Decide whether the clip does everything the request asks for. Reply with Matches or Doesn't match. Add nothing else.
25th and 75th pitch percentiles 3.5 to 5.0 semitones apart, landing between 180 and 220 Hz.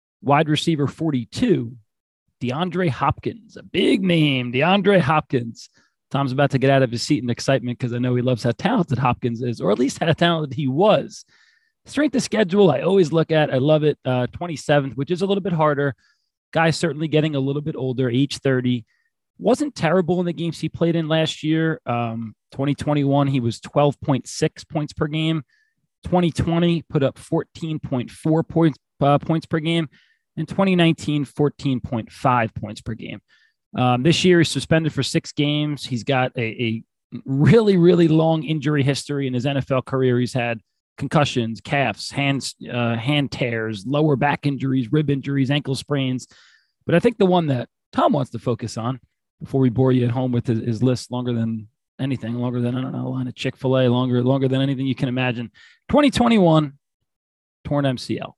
Doesn't match